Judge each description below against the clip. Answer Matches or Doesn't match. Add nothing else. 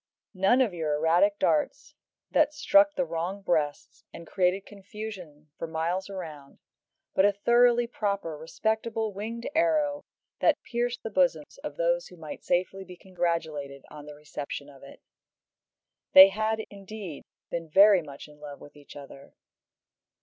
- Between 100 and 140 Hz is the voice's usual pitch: Doesn't match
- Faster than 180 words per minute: Doesn't match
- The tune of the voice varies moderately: Doesn't match